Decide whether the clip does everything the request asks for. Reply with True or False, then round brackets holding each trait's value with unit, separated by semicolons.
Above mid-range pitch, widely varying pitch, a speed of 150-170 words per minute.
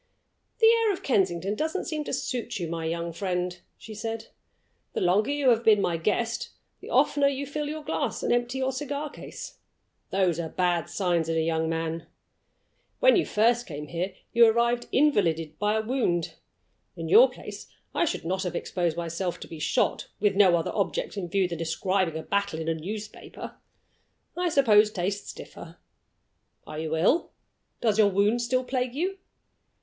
False (205 Hz; 6.8 semitones; 180 wpm)